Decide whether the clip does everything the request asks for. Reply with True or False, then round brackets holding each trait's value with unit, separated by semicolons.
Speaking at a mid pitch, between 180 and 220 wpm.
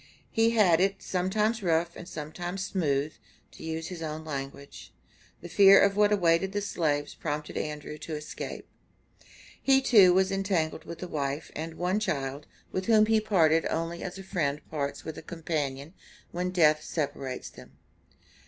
False (170 Hz; 165 wpm)